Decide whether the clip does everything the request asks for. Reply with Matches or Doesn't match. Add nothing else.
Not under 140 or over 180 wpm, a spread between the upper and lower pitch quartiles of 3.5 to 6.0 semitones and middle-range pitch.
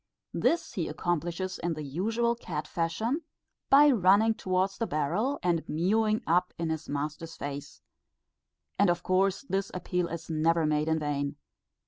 Matches